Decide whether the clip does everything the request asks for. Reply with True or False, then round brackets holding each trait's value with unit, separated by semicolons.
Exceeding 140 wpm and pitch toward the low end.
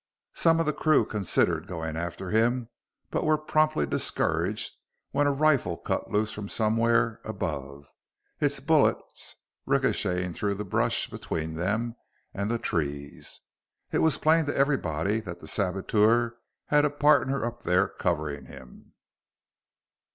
False (135 wpm; 105 Hz)